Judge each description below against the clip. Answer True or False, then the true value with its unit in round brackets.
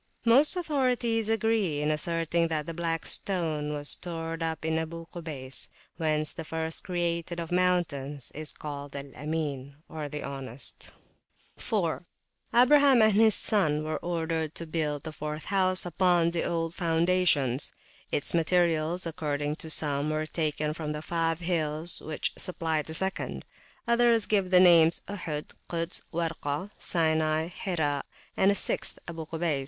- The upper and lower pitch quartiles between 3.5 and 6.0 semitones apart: False (2.8 semitones)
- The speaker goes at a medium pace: True (145 wpm)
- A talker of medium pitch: True (165 Hz)